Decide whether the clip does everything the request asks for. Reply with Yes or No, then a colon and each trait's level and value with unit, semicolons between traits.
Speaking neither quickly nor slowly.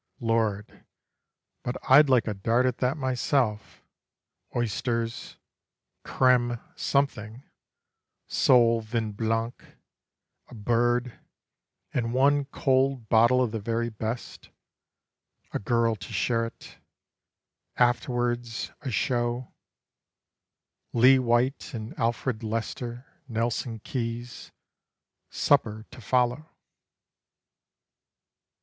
No: slow, 90 wpm